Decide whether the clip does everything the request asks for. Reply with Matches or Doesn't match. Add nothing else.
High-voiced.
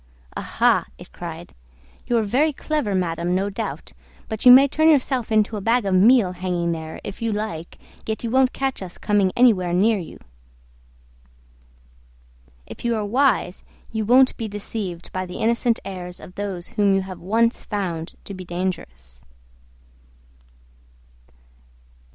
Matches